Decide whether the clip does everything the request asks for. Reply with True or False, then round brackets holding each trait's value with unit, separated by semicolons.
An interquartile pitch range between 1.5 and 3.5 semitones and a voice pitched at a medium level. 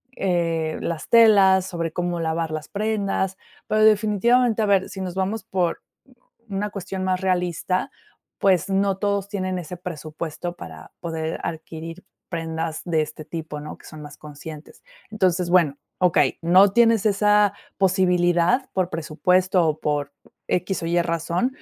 True (3.2 semitones; 180 Hz)